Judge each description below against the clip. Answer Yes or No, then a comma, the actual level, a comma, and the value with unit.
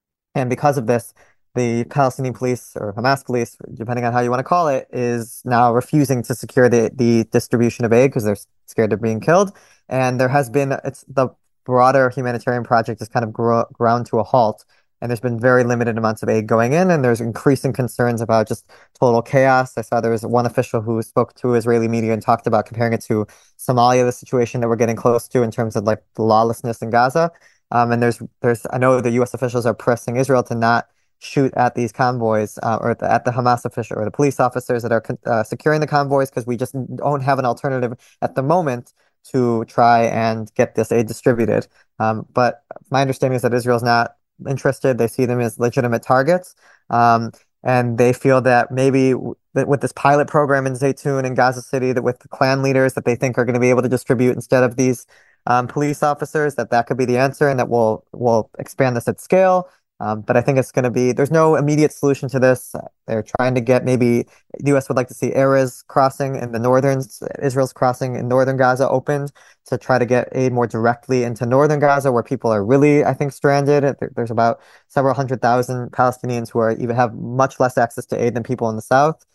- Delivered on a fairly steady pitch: Yes, narrow, 2.3 semitones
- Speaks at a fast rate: Yes, fast, 225 wpm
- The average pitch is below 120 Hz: No, low, 125 Hz